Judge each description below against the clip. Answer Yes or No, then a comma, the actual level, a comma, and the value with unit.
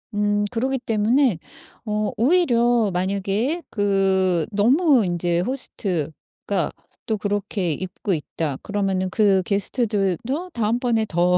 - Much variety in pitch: No, average, 4.0 semitones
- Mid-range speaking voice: No, high, 205 Hz